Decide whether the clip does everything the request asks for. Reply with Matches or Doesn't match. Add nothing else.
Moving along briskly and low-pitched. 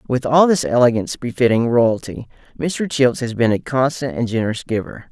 Doesn't match